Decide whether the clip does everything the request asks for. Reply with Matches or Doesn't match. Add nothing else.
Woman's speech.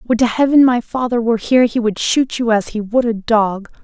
Matches